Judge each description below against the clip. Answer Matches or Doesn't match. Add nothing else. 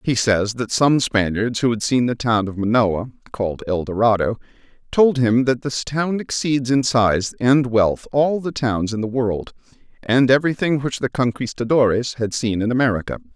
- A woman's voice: Doesn't match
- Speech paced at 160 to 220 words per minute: Matches